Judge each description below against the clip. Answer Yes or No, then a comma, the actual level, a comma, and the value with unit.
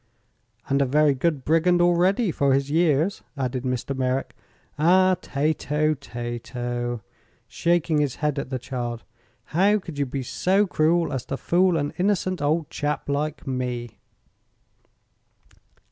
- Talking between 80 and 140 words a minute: Yes, slow, 135 wpm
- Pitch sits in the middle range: Yes, medium, 145 Hz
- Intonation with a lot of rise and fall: No, average, 4.7 semitones